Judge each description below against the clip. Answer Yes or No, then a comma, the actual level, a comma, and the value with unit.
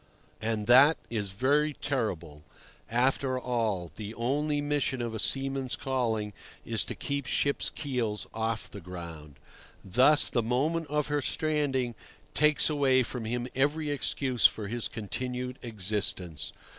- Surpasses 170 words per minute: No, slow, 135 wpm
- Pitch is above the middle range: No, low, 125 Hz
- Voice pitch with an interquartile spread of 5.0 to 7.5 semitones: No, average, 4.5 semitones